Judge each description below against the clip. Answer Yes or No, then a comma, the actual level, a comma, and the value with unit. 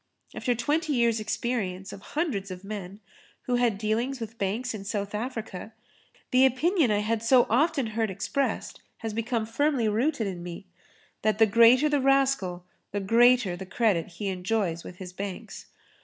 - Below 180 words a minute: Yes, average, 165 wpm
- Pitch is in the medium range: No, high, 225 Hz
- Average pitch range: Yes, average, 4.2 semitones